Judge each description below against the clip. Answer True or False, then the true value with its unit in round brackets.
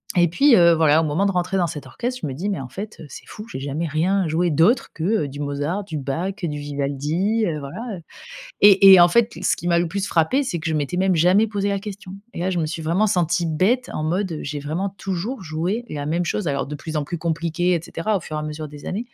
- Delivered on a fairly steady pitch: False (4.1 semitones)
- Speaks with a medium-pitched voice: True (170 Hz)